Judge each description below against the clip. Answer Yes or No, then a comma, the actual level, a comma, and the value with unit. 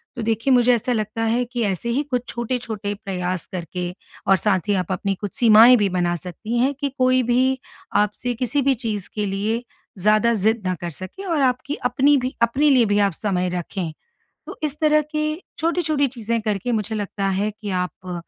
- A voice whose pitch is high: Yes, high, 225 Hz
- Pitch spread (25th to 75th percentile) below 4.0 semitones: No, average, 4.3 semitones